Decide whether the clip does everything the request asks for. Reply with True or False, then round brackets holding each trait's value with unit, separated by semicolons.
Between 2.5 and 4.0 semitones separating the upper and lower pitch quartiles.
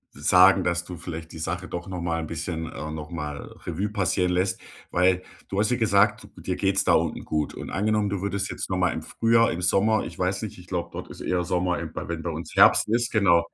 True (2.9 semitones)